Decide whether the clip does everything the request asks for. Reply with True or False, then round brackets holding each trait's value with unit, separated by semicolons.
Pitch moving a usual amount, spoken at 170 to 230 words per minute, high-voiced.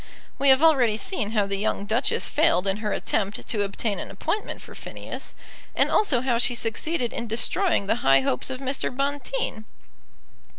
True (5.0 semitones; 175 wpm; 235 Hz)